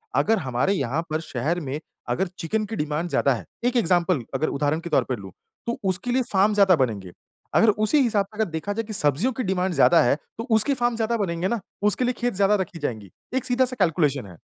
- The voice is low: No, medium, 185 Hz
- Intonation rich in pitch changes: Yes, wide, 6.9 semitones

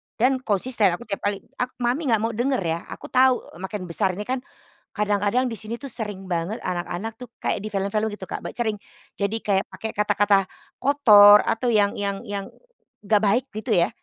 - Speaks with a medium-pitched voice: No, high, 210 Hz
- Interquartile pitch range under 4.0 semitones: Yes, average, 3.2 semitones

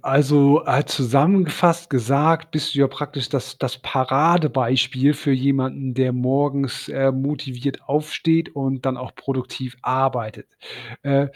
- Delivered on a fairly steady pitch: Yes, narrow, 2.1 semitones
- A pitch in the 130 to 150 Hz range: Yes, low, 135 Hz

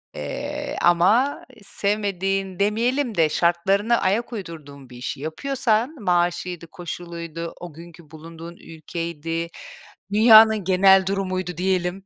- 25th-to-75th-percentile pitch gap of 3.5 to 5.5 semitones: Yes, average, 3.9 semitones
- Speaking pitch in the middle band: Yes, medium, 180 Hz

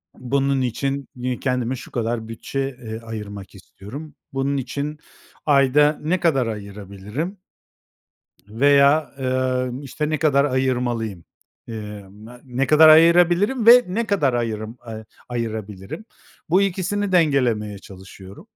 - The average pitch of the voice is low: Yes, low, 130 Hz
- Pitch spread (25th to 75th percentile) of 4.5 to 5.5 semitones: Yes, average, 5.2 semitones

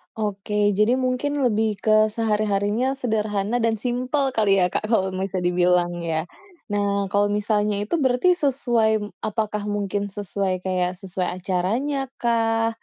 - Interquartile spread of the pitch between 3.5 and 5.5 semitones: No, average, 3.1 semitones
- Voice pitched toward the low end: No, high, 210 Hz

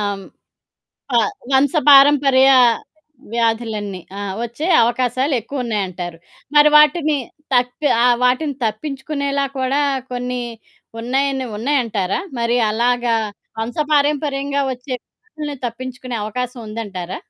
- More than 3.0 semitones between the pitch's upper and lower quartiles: Yes, average, 3.4 semitones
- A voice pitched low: No, very high, 255 Hz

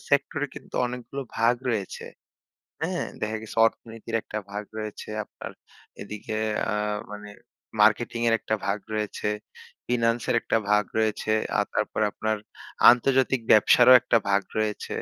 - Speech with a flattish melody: Yes, narrow, 2.2 semitones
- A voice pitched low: Yes, low, 110 Hz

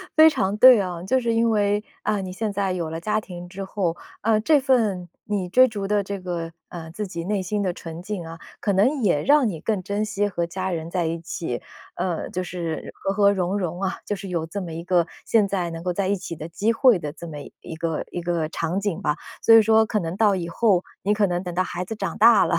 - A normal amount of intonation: Yes, average, 3.4 semitones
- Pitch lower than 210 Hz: Yes, high, 190 Hz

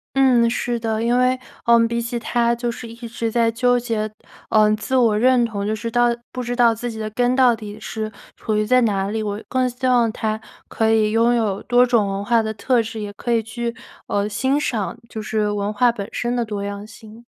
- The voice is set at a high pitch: Yes, high, 230 Hz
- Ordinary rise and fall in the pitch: No, narrow, 2.1 semitones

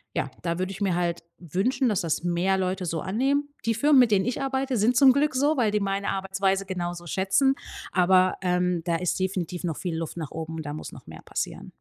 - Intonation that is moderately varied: Yes, average, 4.7 semitones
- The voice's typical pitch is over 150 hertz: Yes, high, 190 Hz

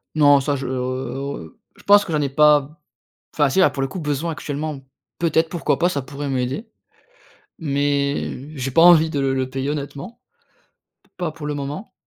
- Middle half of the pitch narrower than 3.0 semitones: Yes, narrow, 2.5 semitones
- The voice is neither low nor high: Yes, medium, 145 Hz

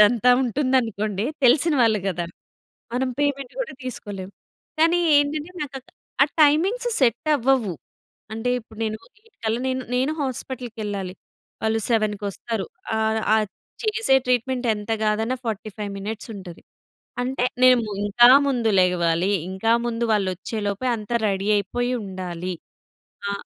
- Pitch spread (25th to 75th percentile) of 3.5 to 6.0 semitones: Yes, average, 4.1 semitones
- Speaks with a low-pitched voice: No, high, 225 Hz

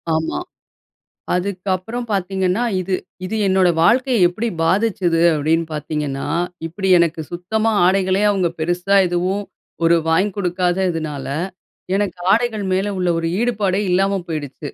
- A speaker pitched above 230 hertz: No, medium, 185 Hz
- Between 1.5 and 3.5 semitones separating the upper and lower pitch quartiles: Yes, average, 2.9 semitones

